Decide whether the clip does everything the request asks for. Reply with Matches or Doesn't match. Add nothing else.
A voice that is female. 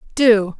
Matches